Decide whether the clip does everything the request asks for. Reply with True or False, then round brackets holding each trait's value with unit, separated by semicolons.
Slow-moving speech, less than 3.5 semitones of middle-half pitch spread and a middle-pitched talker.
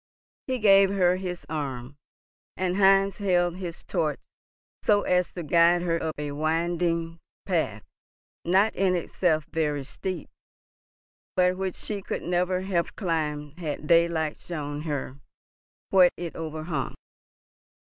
True (125 wpm; 2.8 semitones; 170 Hz)